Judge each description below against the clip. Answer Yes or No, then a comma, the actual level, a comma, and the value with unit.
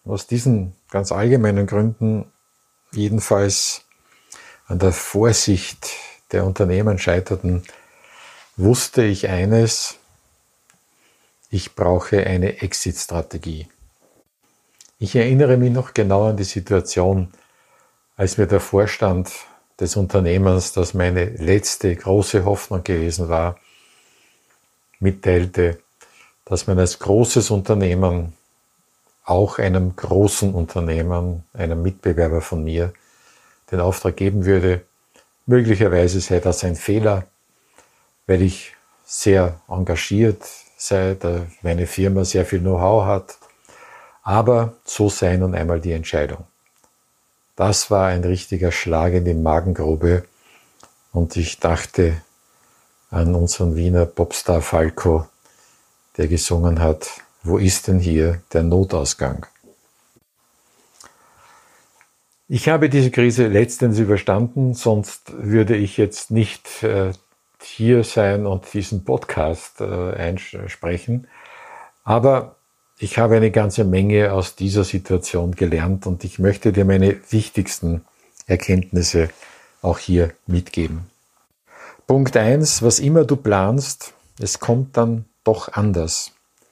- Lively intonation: No, average, 3.8 semitones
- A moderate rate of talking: No, slow, 105 wpm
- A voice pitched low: Yes, very low, 95 Hz